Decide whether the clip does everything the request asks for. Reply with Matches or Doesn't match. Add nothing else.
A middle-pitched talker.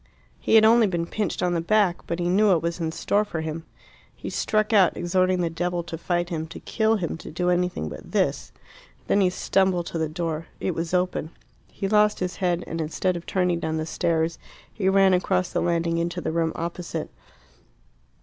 Matches